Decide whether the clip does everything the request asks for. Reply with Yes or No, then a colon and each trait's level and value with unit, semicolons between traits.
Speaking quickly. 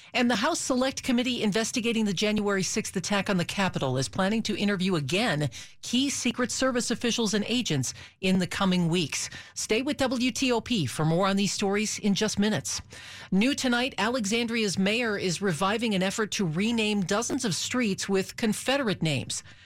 No: average, 170 wpm